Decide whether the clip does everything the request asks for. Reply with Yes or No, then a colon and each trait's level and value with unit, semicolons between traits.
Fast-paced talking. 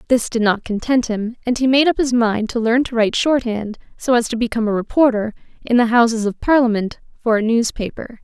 Yes: fast, 220 wpm